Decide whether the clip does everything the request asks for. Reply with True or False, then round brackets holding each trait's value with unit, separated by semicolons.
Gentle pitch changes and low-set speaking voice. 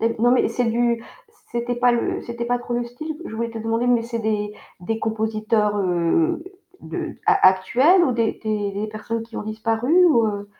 False (2.0 semitones; 230 Hz)